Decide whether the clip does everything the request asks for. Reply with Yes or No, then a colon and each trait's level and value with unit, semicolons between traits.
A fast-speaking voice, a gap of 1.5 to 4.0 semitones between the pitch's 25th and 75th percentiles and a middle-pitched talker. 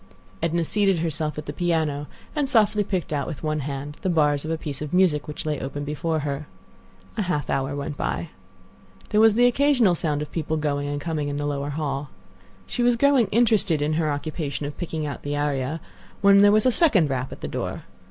No: fast, 215 wpm; average, 4.8 semitones; medium, 155 Hz